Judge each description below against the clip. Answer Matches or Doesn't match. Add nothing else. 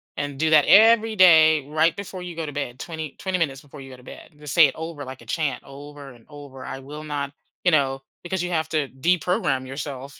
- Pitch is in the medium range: Matches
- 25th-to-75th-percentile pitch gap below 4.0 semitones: Matches